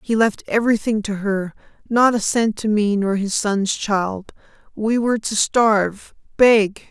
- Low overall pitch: No, high, 210 Hz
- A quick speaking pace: No, average, 140 wpm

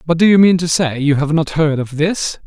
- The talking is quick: Yes, fast, 290 wpm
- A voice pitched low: No, medium, 160 Hz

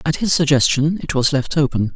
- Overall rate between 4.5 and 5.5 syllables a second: Yes, 5.4 syllables/s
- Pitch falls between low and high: Yes, medium, 145 Hz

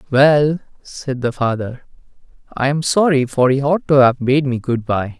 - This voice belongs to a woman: No, male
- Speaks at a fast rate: No, average, 185 wpm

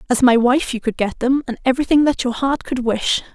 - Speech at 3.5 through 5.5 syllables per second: No, 5.8 syllables/s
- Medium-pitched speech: No, very high, 250 Hz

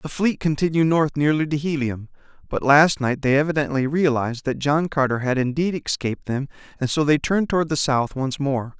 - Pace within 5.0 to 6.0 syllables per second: Yes, 5.5 syllables/s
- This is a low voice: No, medium, 145 Hz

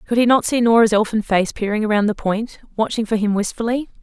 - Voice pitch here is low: No, high, 220 Hz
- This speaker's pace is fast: Yes, fast, 225 wpm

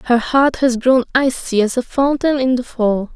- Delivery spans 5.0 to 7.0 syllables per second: No, 4.6 syllables/s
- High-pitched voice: Yes, very high, 250 Hz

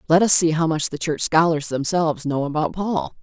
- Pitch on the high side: No, medium, 160 Hz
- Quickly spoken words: Yes, fast, 225 wpm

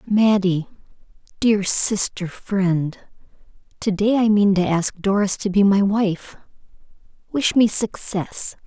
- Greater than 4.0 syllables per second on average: No, 3.6 syllables/s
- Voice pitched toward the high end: Yes, high, 200 Hz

